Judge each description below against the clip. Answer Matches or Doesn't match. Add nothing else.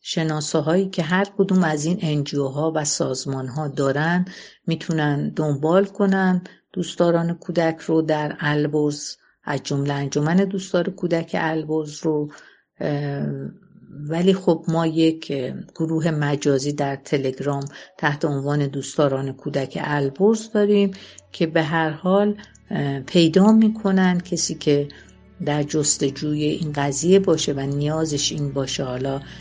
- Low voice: Doesn't match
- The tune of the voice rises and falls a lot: Doesn't match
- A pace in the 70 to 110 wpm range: Doesn't match